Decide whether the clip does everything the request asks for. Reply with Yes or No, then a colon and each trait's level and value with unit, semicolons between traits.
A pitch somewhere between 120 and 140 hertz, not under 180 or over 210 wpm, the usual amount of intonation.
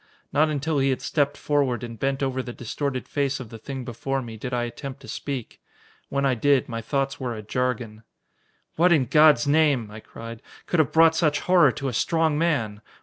Yes: low, 135 Hz; fast, 205 wpm; average, 3.4 semitones